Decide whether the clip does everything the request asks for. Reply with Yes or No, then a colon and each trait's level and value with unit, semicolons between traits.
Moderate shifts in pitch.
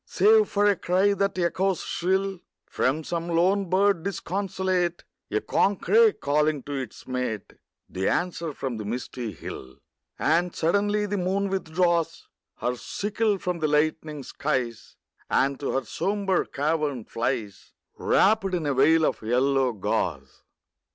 No: wide, 6.0 semitones